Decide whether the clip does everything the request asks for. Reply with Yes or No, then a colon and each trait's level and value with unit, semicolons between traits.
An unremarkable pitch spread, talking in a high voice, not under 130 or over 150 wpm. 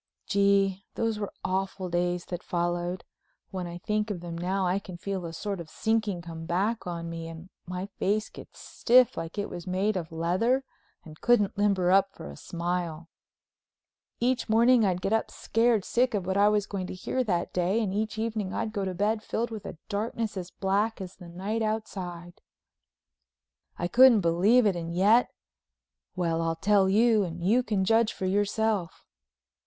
No: average, 3.6 semitones; high, 195 Hz; average, 180 wpm